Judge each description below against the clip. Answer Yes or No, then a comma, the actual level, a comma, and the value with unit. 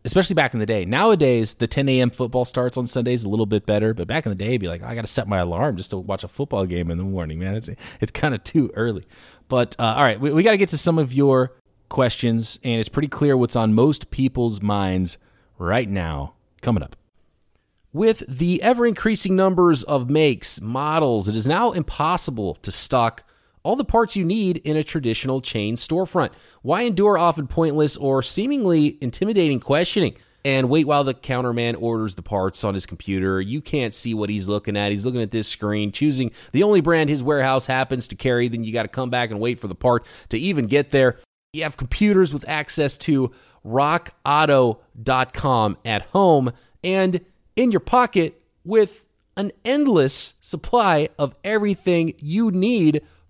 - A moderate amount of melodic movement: No, wide, 6.5 semitones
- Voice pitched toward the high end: No, low, 130 Hz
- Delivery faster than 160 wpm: Yes, average, 195 wpm